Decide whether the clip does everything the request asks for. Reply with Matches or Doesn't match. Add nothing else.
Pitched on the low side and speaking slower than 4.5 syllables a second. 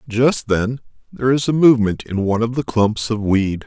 Doesn't match